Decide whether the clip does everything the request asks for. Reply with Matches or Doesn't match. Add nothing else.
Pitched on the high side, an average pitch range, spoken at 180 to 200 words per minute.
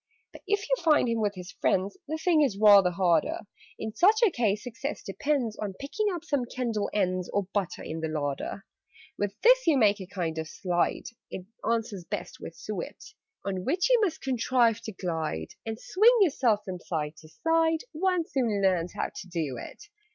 Doesn't match